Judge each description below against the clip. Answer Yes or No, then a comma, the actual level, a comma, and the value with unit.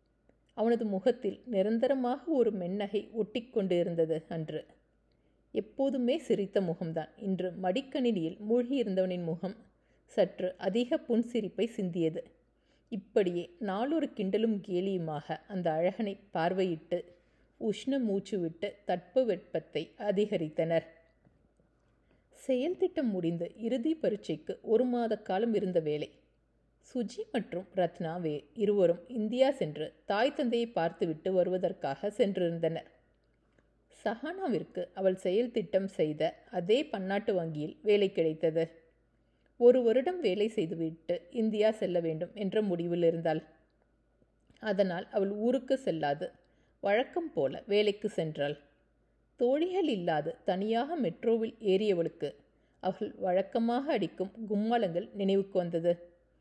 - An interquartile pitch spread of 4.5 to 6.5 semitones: Yes, average, 5.1 semitones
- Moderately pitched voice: No, high, 195 Hz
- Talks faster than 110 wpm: No, average, 95 wpm